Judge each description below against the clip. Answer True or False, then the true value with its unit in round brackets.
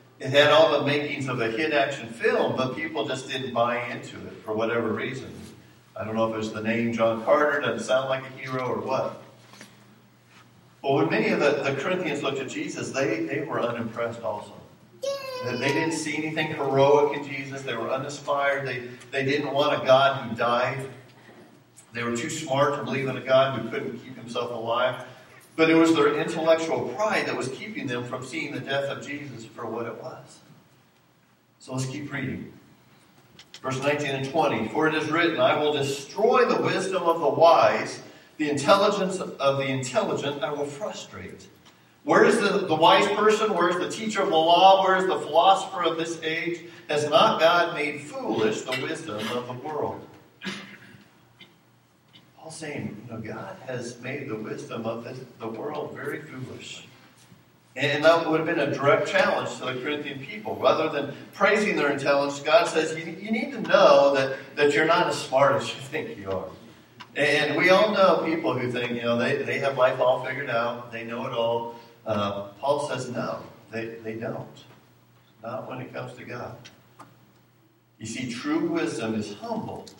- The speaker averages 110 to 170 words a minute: False (190 wpm)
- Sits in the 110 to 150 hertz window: True (135 Hz)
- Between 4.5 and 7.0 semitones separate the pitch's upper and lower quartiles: True (5.0 semitones)